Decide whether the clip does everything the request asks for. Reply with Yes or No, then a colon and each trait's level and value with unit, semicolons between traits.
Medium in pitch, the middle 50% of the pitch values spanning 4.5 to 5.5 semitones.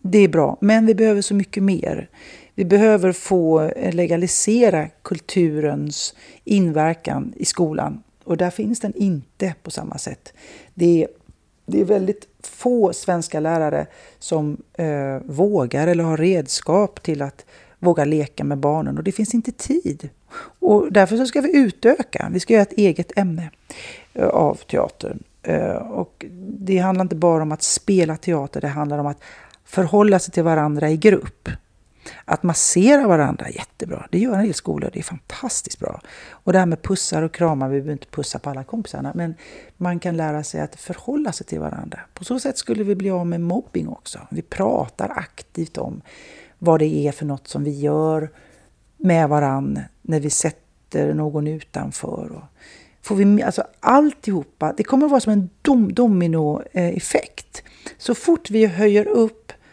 Yes: medium, 180 Hz; average, 5.0 semitones